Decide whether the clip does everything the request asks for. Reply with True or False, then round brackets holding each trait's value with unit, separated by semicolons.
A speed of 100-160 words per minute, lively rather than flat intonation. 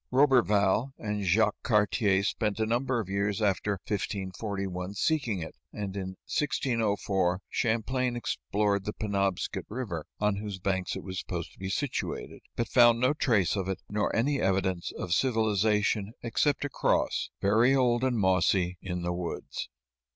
False (150 wpm; 3.6 semitones)